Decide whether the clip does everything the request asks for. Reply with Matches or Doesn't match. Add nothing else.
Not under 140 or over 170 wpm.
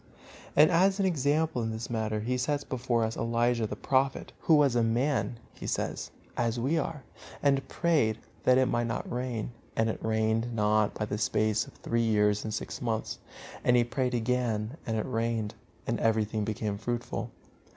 Doesn't match